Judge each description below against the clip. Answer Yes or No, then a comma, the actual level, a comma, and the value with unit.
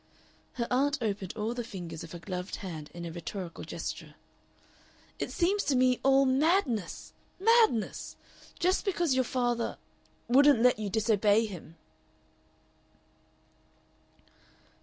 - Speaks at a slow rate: Yes, slow, 120 wpm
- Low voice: No, high, 235 Hz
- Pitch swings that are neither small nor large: No, wide, 6.1 semitones